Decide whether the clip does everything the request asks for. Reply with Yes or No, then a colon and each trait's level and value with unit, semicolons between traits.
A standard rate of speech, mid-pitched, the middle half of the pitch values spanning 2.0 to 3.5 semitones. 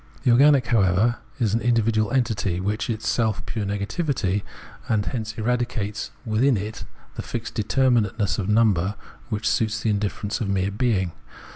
No: average, 150 wpm; low, 110 Hz; average, 2.7 semitones